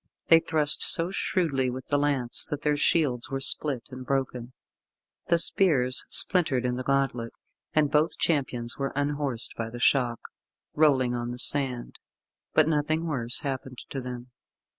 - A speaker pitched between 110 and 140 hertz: Yes, low, 135 Hz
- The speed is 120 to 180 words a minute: Yes, average, 155 wpm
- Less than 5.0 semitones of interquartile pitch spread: Yes, average, 3.2 semitones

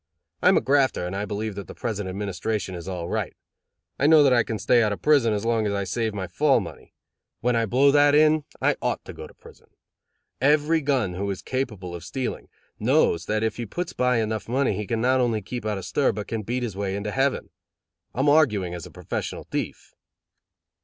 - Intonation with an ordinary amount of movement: Yes, average, 4.9 semitones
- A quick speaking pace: Yes, fast, 225 wpm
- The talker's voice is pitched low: Yes, low, 110 Hz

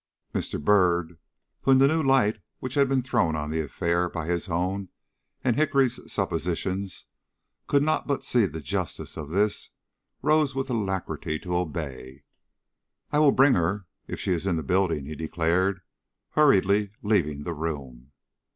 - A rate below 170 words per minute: Yes, average, 160 wpm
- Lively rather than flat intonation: Yes, wide, 7.6 semitones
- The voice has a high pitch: No, very low, 95 Hz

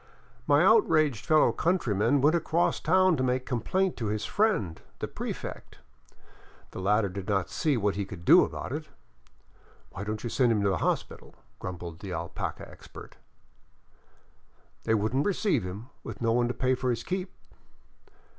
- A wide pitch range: Yes, wide, 7.5 semitones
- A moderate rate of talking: Yes, average, 170 wpm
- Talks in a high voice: No, low, 120 Hz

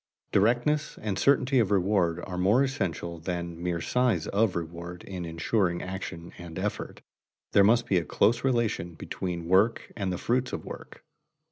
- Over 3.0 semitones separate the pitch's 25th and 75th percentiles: Yes, average, 5.0 semitones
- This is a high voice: No, very low, 95 Hz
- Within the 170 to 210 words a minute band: No, average, 160 wpm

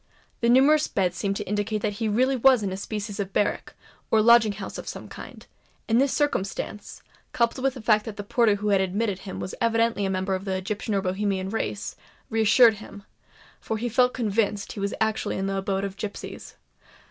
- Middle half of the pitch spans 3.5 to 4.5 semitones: No, average, 2.7 semitones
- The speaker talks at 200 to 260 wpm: Yes, fast, 205 wpm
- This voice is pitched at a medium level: No, high, 210 Hz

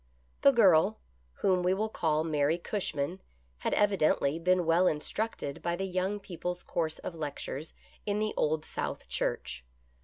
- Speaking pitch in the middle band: Yes, medium, 175 Hz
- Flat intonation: No, average, 3.7 semitones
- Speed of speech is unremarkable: Yes, average, 155 wpm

